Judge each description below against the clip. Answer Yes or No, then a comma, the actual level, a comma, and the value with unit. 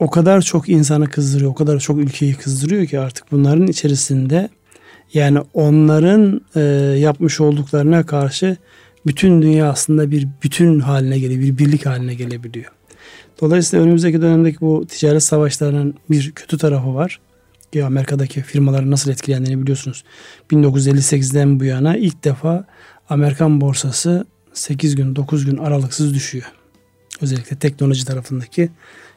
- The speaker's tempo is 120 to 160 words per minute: Yes, average, 130 wpm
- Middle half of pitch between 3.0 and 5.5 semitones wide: No, narrow, 2.4 semitones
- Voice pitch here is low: No, medium, 145 Hz